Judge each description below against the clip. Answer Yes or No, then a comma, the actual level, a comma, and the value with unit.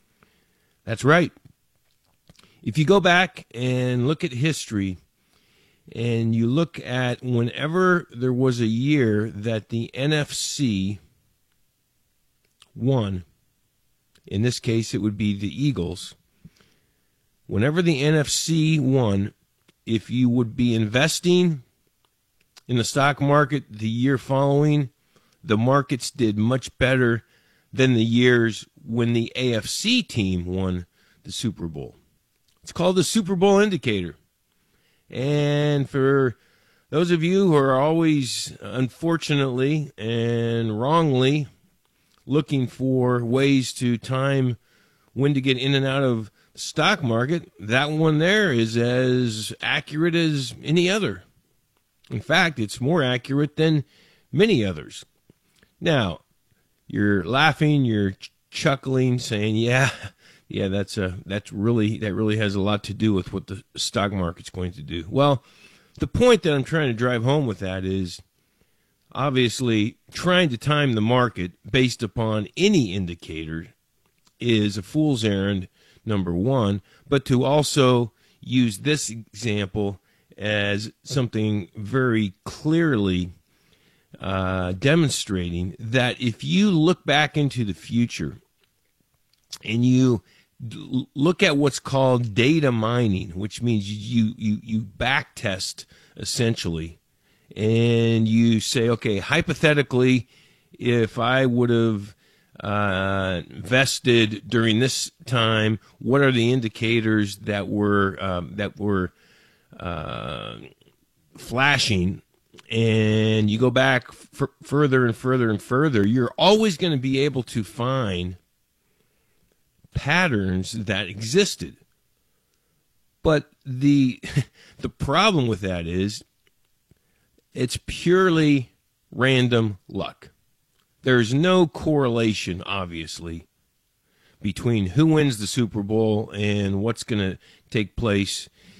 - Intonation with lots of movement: No, average, 4.9 semitones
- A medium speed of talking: No, slow, 120 wpm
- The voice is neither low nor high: No, low, 120 Hz